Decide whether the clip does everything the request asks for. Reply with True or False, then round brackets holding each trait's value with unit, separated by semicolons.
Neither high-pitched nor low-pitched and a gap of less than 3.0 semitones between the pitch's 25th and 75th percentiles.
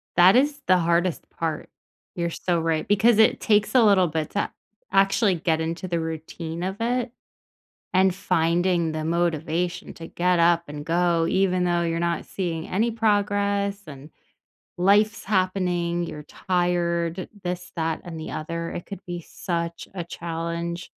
True (175 Hz; 2.4 semitones)